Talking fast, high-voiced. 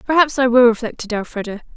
No: average, 170 wpm; high, 240 Hz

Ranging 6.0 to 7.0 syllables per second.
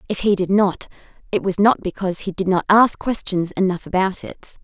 No: 5.3 syllables/s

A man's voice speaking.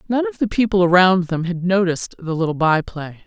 No: female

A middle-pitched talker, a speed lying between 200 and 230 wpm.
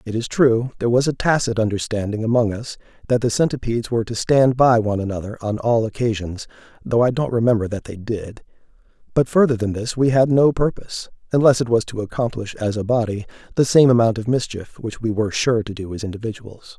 No: low, 115 Hz; fast, 205 wpm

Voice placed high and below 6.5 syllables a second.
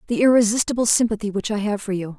No: high, 215 Hz; 7.0 syllables/s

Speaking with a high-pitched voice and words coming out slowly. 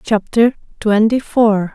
Yes: high, 220 Hz; slow, 105 wpm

